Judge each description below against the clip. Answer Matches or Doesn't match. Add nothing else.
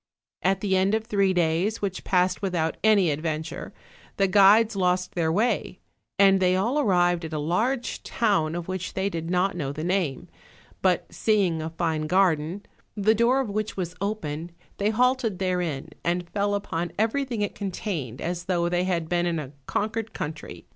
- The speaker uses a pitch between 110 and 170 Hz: Doesn't match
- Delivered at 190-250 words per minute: Doesn't match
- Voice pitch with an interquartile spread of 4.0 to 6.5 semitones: Doesn't match